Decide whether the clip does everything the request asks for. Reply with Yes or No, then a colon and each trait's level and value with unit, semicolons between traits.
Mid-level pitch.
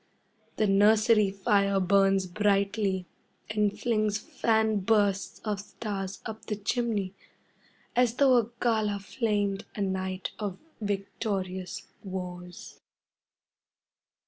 No: high, 205 Hz